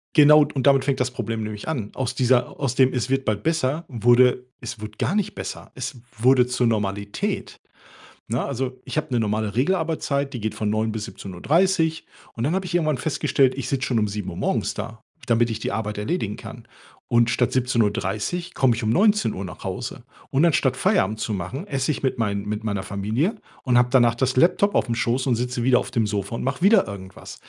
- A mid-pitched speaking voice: No, low, 125 Hz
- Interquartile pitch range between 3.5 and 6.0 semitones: Yes, average, 4.0 semitones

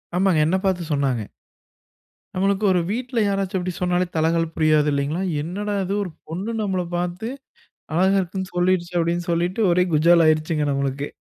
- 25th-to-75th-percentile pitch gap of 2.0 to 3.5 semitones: Yes, average, 3.0 semitones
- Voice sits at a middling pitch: Yes, medium, 175 Hz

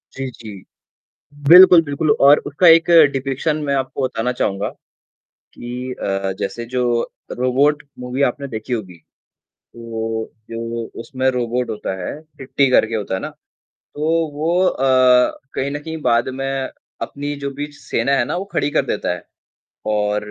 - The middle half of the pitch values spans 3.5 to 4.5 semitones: Yes, average, 3.9 semitones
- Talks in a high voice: No, low, 130 Hz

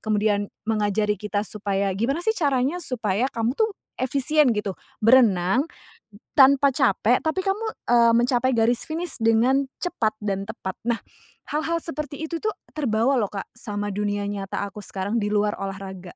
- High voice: Yes, high, 230 Hz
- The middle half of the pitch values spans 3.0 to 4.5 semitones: No, average, 5.1 semitones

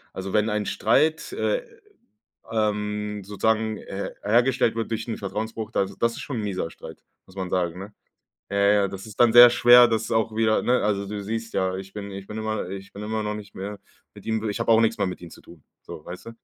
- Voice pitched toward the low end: Yes, low, 105 Hz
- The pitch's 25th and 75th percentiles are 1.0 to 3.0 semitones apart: Yes, narrow, 2.4 semitones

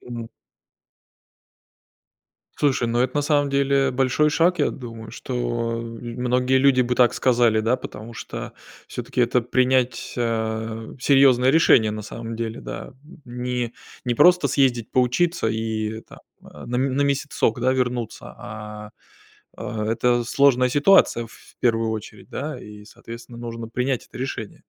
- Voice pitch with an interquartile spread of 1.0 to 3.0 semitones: Yes, narrow, 2.5 semitones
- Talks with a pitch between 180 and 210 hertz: No, low, 120 Hz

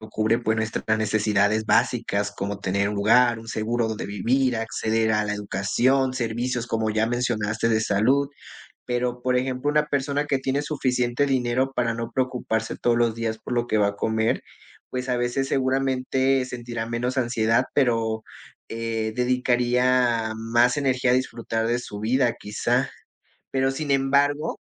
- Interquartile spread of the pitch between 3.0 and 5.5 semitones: No, narrow, 2.6 semitones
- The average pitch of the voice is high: No, low, 120 Hz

